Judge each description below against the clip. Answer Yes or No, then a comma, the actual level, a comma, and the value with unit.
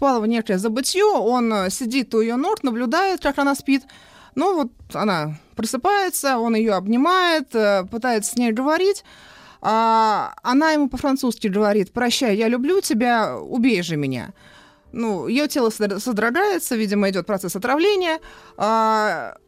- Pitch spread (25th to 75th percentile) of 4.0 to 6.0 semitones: Yes, average, 4.5 semitones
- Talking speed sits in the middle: Yes, average, 135 wpm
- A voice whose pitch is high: Yes, high, 240 Hz